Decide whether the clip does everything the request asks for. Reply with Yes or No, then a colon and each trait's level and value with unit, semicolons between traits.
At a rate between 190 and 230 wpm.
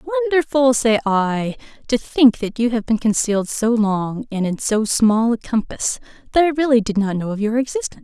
Yes: average, 200 wpm